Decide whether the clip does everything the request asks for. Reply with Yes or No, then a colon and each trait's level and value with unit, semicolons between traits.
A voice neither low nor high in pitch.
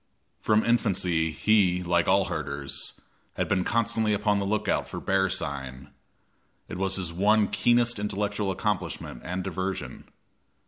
No: very low, 95 Hz